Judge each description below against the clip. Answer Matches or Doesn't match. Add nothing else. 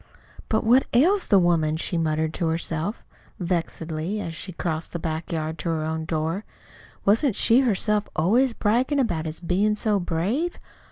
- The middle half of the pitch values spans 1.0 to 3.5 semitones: Doesn't match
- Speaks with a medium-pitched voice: Matches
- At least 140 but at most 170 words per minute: Matches